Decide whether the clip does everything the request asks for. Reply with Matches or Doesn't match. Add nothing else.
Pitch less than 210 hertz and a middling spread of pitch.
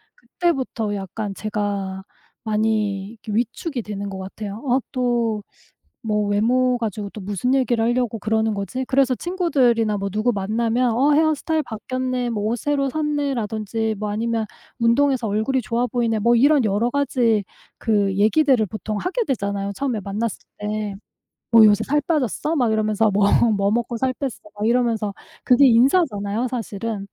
Doesn't match